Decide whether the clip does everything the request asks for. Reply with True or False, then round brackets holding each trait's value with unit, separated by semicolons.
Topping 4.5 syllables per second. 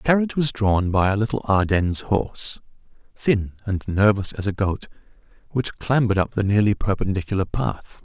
True (5.4 syllables/s)